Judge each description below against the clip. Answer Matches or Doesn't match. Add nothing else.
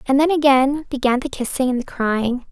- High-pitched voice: Matches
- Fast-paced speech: Matches